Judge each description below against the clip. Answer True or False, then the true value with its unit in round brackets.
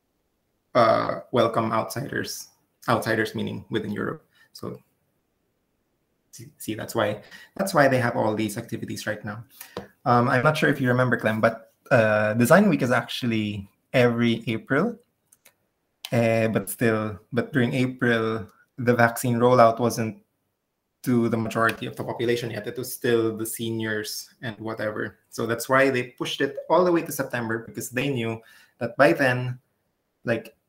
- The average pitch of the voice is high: False (115 Hz)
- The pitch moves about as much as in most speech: False (2.2 semitones)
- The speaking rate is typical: True (155 wpm)